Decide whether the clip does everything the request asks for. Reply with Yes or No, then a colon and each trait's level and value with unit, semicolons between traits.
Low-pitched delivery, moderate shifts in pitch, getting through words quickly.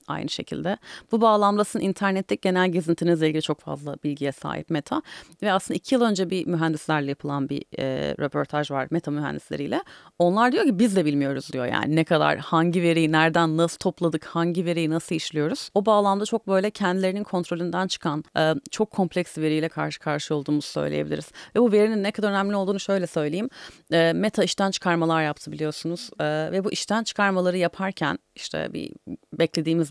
No: medium, 170 Hz; average, 4.0 semitones; fast, 170 wpm